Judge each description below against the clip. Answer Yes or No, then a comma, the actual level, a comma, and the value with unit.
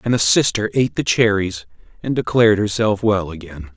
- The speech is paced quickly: No, average, 175 wpm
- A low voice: Yes, low, 105 Hz